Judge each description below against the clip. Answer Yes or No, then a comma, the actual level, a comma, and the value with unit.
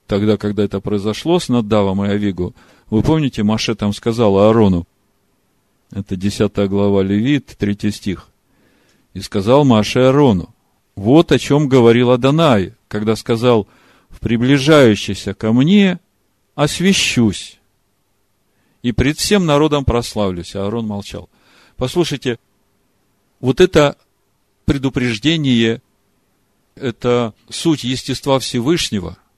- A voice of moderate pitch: No, low, 110 Hz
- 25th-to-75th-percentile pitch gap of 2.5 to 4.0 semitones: No, average, 4.7 semitones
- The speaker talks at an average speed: No, slow, 105 wpm